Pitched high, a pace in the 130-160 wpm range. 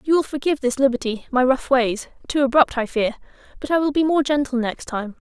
No: very high, 265 Hz; fast, 205 wpm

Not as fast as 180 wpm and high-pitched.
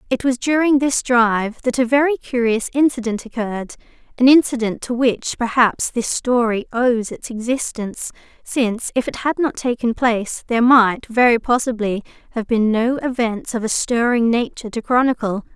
Yes: average, 160 wpm; high, 240 Hz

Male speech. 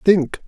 Yes: male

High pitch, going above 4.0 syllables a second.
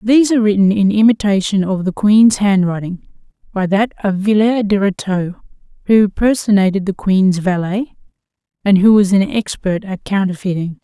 Yes: high, 200 Hz; 5.0 syllables/s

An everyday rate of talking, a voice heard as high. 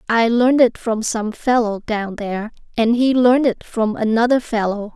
Yes: average, 180 wpm; high, 230 Hz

